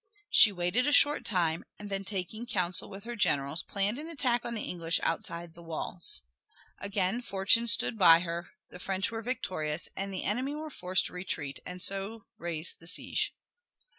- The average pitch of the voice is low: No, high, 195 Hz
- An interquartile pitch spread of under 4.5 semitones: No, average, 4.8 semitones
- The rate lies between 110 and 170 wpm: No, average, 180 wpm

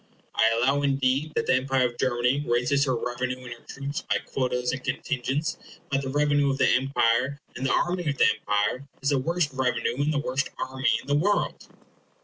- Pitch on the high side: No, low, 135 Hz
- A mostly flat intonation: Yes, narrow, 2.2 semitones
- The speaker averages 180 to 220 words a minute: Yes, average, 200 wpm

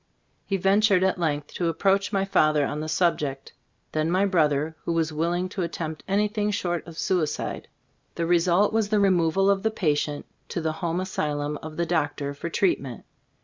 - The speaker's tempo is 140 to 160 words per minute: No, average, 185 wpm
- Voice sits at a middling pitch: Yes, medium, 170 Hz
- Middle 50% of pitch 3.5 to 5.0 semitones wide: Yes, average, 3.9 semitones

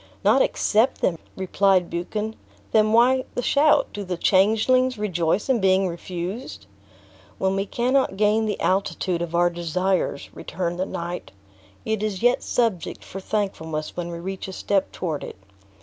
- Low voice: No, high, 190 Hz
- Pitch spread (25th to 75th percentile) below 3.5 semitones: No, average, 3.8 semitones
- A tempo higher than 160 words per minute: No, average, 155 wpm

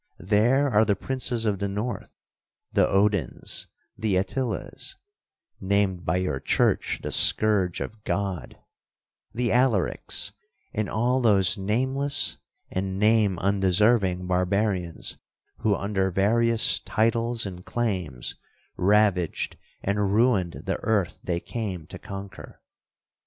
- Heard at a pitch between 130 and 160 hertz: No, low, 100 Hz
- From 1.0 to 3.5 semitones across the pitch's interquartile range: Yes, average, 3.2 semitones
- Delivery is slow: Yes, slow, 115 wpm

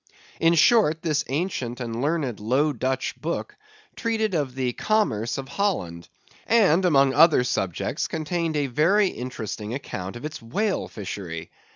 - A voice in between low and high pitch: Yes, medium, 145 Hz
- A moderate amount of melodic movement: No, wide, 6.1 semitones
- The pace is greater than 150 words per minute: No, average, 145 wpm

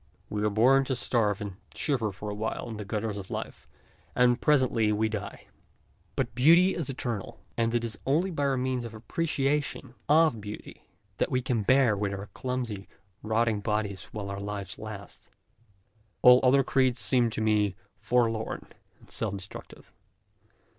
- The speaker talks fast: No, average, 165 wpm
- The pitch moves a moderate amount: Yes, average, 3.7 semitones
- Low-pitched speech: Yes, low, 115 Hz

